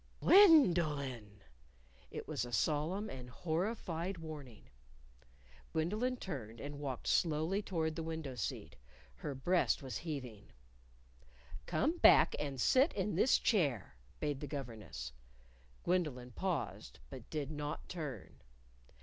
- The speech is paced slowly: Yes, slow, 125 wpm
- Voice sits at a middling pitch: Yes, medium, 150 Hz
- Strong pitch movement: Yes, wide, 5.8 semitones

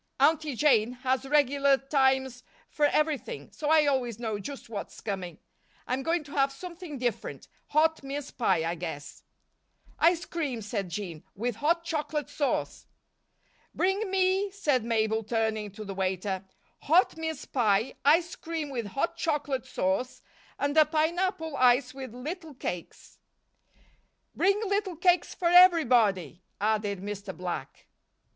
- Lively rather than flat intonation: Yes, wide, 6.7 semitones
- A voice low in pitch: No, very high, 270 Hz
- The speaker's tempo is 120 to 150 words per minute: Yes, average, 140 wpm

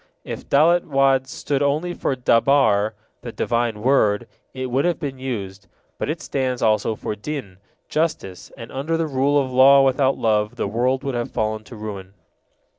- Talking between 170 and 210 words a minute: Yes, average, 175 wpm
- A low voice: Yes, low, 130 Hz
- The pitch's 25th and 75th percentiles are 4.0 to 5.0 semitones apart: Yes, average, 4.4 semitones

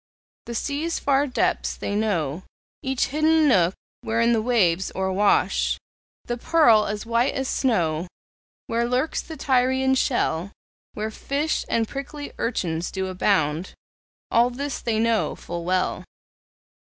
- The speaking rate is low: Yes, slow, 130 wpm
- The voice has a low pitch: No, high, 230 Hz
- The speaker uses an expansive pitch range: Yes, wide, 5.8 semitones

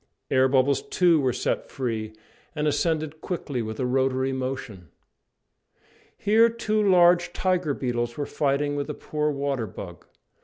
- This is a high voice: No, medium, 140 Hz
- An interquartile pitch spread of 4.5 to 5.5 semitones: No, average, 4.1 semitones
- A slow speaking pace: No, average, 145 wpm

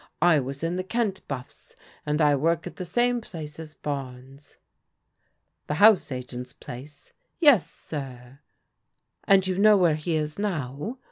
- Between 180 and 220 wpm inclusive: No, average, 165 wpm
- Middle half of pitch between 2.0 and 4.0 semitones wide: No, wide, 5.5 semitones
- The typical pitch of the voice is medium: Yes, medium, 155 Hz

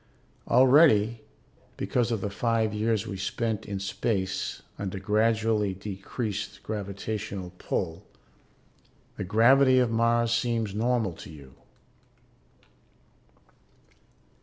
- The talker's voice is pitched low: Yes, low, 110 Hz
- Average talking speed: No, slow, 95 wpm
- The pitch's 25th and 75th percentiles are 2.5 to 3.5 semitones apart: Yes, average, 2.9 semitones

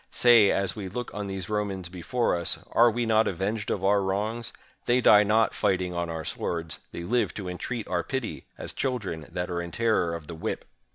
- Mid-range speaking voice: No, low, 100 Hz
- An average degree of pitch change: Yes, average, 4.2 semitones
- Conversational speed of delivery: No, fast, 210 wpm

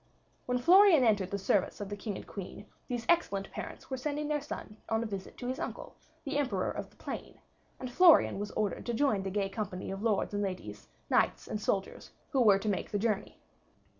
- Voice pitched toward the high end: Yes, high, 215 Hz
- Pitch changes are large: No, average, 4.7 semitones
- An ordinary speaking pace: No, fast, 215 wpm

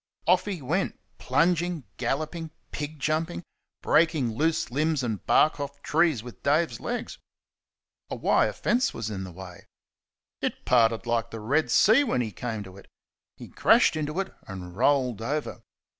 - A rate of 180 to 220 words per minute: No, average, 160 wpm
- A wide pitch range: Yes, wide, 6.1 semitones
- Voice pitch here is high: No, medium, 145 Hz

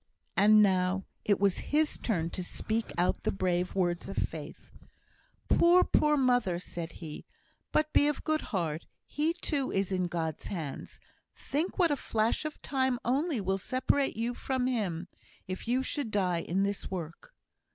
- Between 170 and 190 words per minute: No, average, 160 wpm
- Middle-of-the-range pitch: No, high, 200 Hz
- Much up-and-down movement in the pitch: Yes, wide, 6.7 semitones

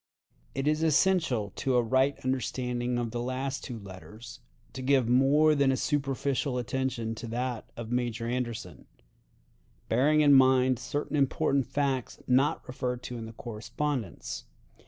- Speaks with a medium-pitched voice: No, low, 130 Hz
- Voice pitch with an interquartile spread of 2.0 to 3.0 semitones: Yes, narrow, 2.6 semitones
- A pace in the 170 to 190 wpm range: No, average, 145 wpm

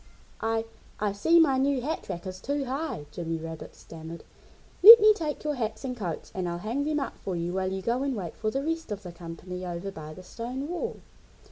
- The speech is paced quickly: Yes, fast, 225 wpm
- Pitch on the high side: Yes, high, 215 Hz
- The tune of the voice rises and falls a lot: Yes, wide, 7.9 semitones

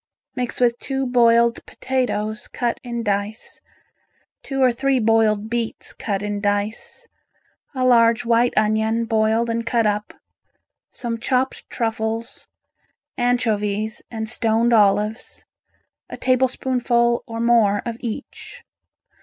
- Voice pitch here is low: No, high, 230 Hz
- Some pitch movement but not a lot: No, narrow, 1.9 semitones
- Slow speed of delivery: Yes, slow, 115 wpm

